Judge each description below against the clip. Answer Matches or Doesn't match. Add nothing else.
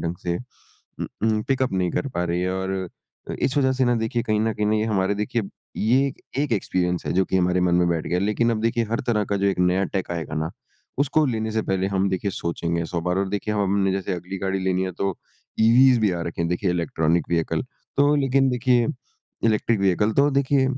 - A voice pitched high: Doesn't match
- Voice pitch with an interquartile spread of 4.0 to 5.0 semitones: Matches